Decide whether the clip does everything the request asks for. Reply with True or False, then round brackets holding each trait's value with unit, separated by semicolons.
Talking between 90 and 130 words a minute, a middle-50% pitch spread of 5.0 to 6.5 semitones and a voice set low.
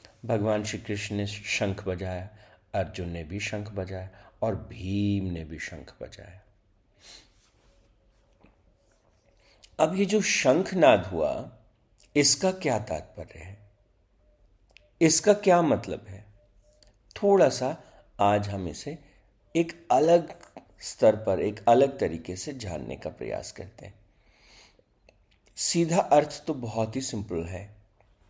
False (120 wpm; 2.4 semitones; 105 Hz)